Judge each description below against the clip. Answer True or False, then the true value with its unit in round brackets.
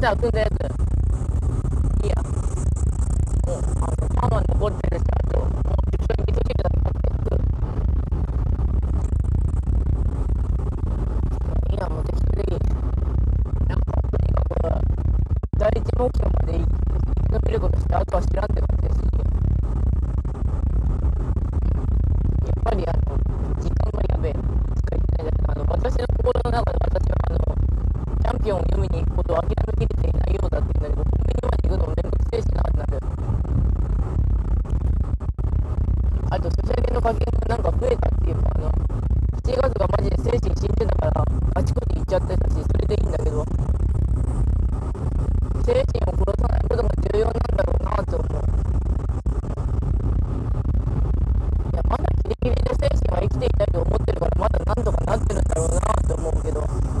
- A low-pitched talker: True (85 Hz)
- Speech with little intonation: True (2.3 semitones)